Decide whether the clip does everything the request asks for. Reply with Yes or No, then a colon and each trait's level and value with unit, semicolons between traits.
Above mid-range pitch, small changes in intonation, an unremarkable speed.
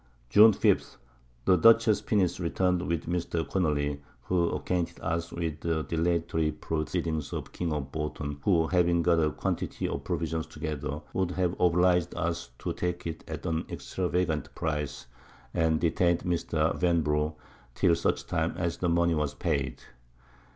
No: very low, 85 Hz; narrow, 2.2 semitones; average, 150 wpm